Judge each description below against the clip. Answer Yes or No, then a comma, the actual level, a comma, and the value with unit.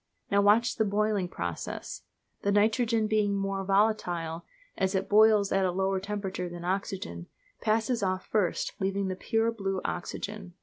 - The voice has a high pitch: Yes, high, 200 Hz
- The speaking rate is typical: Yes, average, 150 wpm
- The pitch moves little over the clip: Yes, narrow, 2.3 semitones